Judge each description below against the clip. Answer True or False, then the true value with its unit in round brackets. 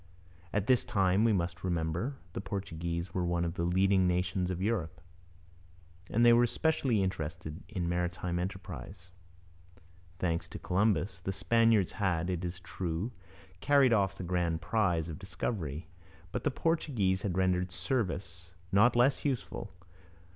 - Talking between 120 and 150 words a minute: True (145 wpm)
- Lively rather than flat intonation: False (3.7 semitones)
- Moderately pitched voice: False (95 Hz)